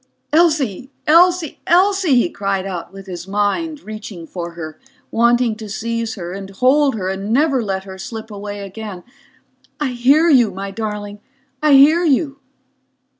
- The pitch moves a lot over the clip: Yes, wide, 6.3 semitones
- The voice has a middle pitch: No, high, 220 Hz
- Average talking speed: Yes, average, 155 wpm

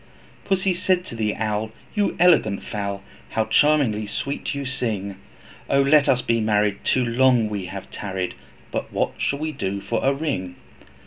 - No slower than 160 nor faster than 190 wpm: Yes, average, 170 wpm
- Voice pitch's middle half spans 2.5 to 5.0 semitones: No, wide, 5.4 semitones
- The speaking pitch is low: Yes, low, 115 Hz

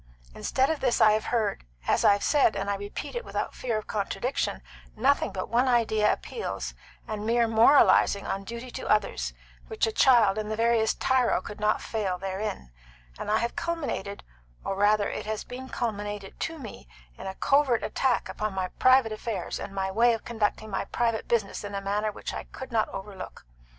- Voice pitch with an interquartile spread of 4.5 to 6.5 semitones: No, average, 2.9 semitones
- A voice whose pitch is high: Yes, high, 215 Hz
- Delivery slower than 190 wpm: No, average, 195 wpm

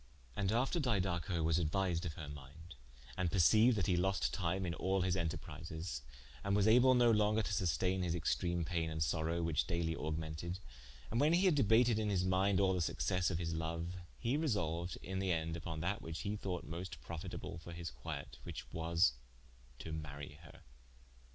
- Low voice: Yes, very low, 85 Hz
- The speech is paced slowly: No, average, 190 wpm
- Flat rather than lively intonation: No, average, 3.3 semitones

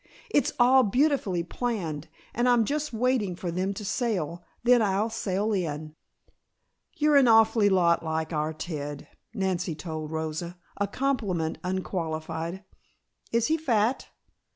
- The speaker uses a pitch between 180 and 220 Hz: Yes, high, 190 Hz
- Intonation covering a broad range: Yes, wide, 6.3 semitones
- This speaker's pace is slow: Yes, slow, 130 wpm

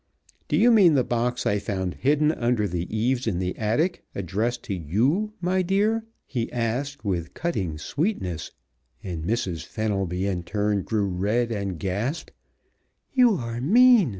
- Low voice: Yes, low, 115 Hz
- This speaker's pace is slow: No, average, 150 wpm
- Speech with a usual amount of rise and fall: No, wide, 7.6 semitones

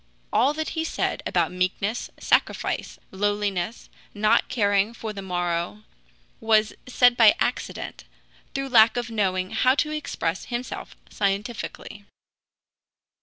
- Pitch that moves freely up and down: No, average, 3.8 semitones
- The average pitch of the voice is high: Yes, high, 215 Hz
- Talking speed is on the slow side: Yes, slow, 120 wpm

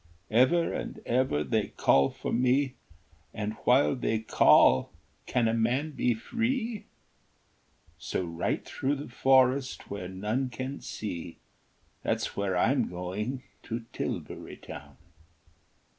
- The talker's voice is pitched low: Yes, low, 125 Hz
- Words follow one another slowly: Yes, slow, 120 wpm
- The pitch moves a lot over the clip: No, average, 4.5 semitones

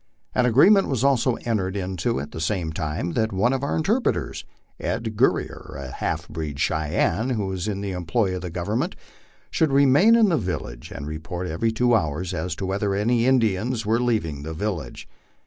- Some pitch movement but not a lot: No, wide, 6.6 semitones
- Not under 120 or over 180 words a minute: No, average, 190 wpm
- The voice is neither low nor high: No, low, 100 Hz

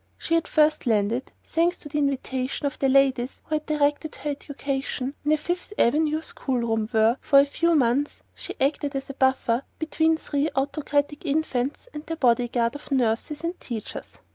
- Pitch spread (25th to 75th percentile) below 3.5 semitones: Yes, average, 3.0 semitones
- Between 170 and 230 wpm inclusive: Yes, average, 180 wpm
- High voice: Yes, very high, 280 Hz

